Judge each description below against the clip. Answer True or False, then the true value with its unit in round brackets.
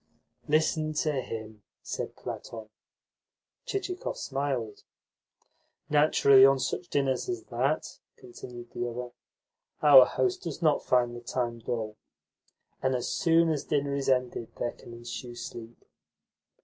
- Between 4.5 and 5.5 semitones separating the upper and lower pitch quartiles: False (4.1 semitones)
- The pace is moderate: False (125 wpm)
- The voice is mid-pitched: False (130 Hz)